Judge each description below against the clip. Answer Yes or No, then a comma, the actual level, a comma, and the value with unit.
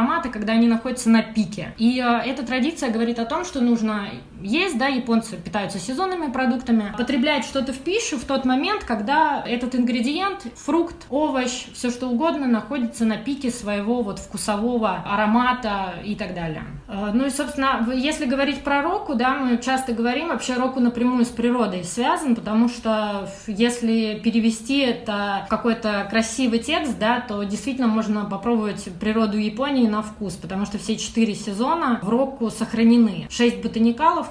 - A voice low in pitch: No, high, 235 Hz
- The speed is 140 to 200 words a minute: Yes, average, 155 wpm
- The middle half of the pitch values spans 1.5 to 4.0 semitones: Yes, average, 3.4 semitones